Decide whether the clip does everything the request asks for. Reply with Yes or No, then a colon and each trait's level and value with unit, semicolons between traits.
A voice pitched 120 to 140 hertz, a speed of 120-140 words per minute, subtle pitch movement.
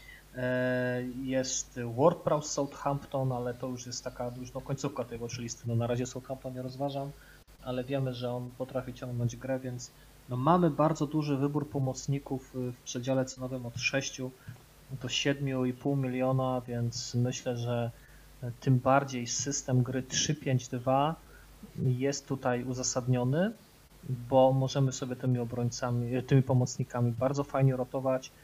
Yes: low, 130 Hz; average, 135 wpm; narrow, 1.8 semitones